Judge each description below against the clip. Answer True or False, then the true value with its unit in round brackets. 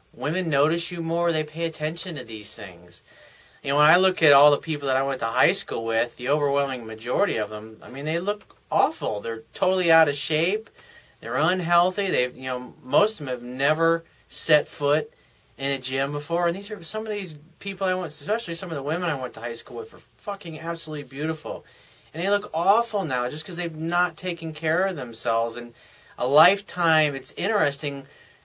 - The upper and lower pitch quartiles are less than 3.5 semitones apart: False (4.2 semitones)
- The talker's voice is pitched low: False (155 Hz)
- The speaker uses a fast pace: True (210 wpm)